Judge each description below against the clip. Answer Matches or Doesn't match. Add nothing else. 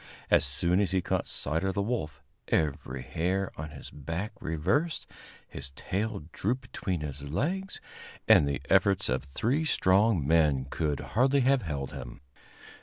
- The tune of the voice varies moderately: Doesn't match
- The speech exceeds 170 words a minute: Doesn't match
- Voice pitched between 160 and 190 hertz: Doesn't match